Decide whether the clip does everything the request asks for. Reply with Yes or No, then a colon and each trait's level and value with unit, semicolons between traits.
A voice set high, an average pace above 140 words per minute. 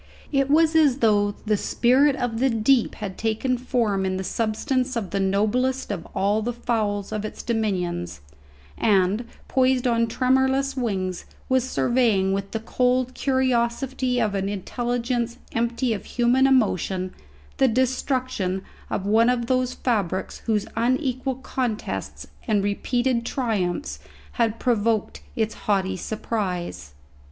No: high, 230 Hz; slow, 135 wpm